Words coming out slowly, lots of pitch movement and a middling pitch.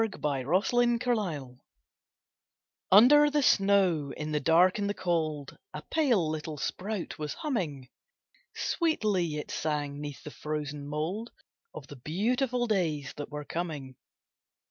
Yes: slow, 130 wpm; wide, 6.3 semitones; medium, 165 Hz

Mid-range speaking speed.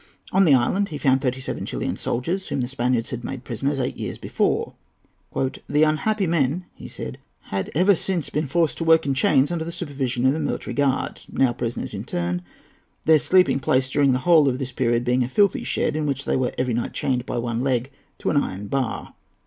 No: fast, 215 wpm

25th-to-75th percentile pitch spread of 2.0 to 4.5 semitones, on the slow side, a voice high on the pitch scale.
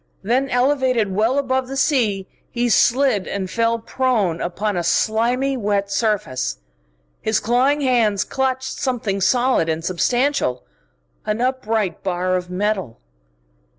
No: average, 5.0 semitones; slow, 125 wpm; high, 225 Hz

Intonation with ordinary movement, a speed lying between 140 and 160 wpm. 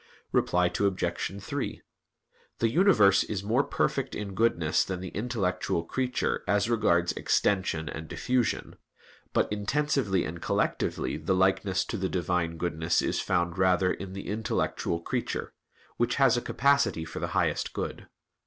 Yes: average, 4.2 semitones; average, 145 wpm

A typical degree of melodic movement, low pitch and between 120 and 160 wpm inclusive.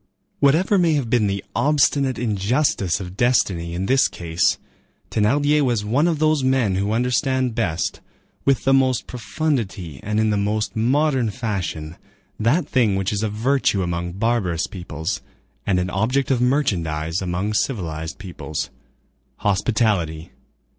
No: wide, 6.2 semitones; low, 110 Hz; average, 140 wpm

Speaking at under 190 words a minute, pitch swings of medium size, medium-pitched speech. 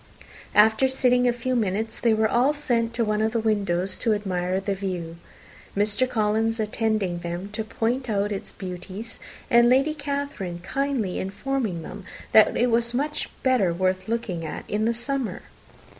No: average, 165 wpm; average, 4.0 semitones; high, 220 Hz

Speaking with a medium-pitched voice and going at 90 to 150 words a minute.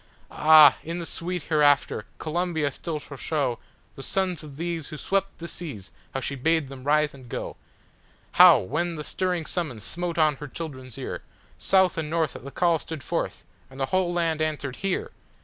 No: medium, 155 Hz; average, 175 wpm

